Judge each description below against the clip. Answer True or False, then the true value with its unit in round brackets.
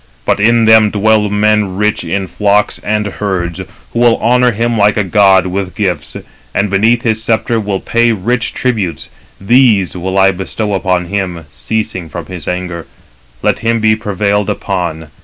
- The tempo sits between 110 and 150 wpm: False (165 wpm)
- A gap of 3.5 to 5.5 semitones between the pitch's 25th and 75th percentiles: False (3.1 semitones)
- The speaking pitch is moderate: False (105 Hz)